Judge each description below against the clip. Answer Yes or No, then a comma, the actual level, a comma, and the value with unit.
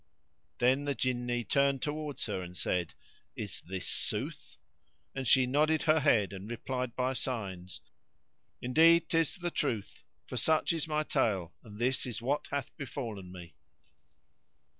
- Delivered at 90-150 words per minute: Yes, average, 145 wpm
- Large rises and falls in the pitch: Yes, wide, 5.9 semitones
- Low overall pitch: Yes, low, 125 Hz